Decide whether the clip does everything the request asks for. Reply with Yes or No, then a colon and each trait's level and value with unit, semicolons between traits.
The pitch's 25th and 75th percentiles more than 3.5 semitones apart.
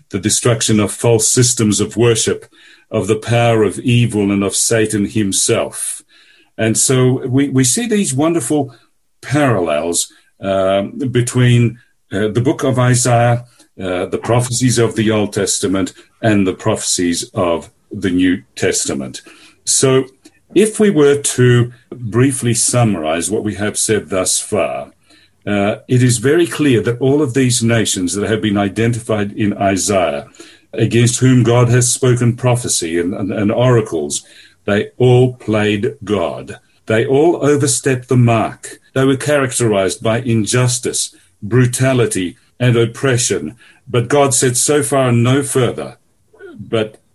No: average, 3.2 semitones